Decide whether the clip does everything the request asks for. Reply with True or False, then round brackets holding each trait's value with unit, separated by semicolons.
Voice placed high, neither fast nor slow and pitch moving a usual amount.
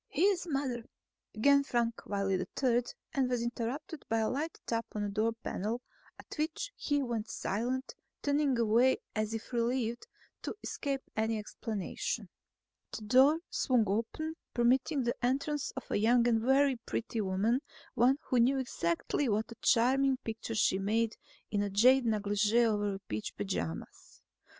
True (235 Hz; 150 wpm; 3.5 semitones)